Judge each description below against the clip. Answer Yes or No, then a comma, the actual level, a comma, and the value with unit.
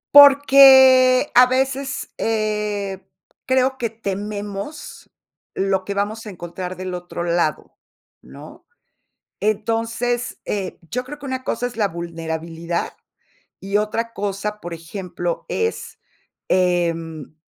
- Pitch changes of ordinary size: No, wide, 5.8 semitones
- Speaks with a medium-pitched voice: No, high, 205 Hz